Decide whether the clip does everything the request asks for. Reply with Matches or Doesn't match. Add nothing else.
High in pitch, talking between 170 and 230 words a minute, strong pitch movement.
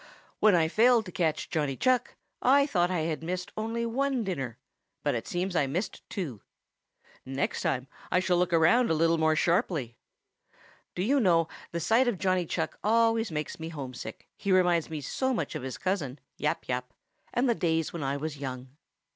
Doesn't match